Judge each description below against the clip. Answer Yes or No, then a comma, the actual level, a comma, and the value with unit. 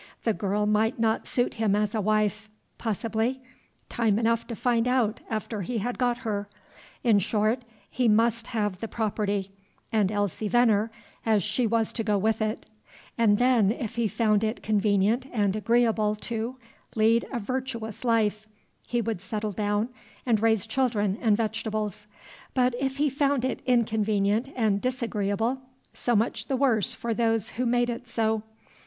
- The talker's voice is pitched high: Yes, high, 220 Hz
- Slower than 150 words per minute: No, average, 160 wpm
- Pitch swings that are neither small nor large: No, narrow, 2.1 semitones